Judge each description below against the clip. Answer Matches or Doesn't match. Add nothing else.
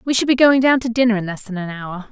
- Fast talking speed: Matches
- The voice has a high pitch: Matches